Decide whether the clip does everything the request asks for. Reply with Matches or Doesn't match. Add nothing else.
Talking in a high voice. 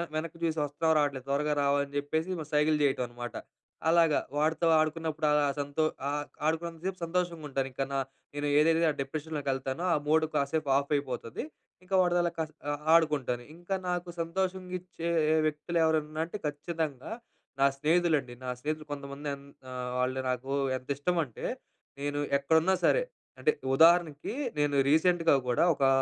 Doesn't match